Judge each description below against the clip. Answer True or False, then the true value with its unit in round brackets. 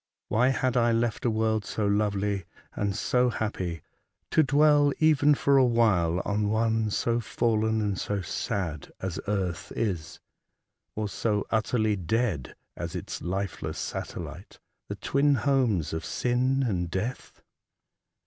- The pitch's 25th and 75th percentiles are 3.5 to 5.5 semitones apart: True (3.9 semitones)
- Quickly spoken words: False (145 wpm)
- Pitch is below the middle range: True (110 Hz)